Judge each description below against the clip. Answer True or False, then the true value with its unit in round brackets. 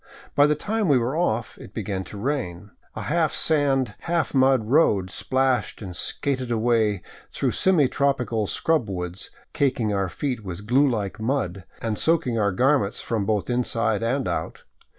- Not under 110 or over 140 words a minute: False (165 wpm)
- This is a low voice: True (120 Hz)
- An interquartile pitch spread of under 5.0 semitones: False (5.3 semitones)